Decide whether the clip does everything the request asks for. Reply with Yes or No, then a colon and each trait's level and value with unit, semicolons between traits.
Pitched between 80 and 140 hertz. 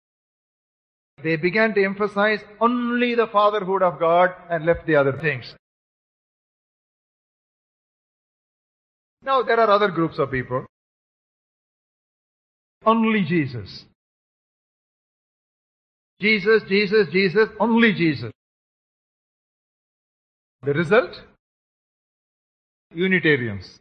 No: medium, 185 Hz